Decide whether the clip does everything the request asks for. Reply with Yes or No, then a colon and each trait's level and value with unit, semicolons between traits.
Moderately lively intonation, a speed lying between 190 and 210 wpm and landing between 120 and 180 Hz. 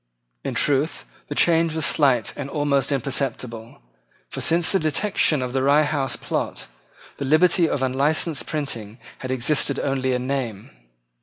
No: average, 3.0 semitones; average, 150 wpm; medium, 140 Hz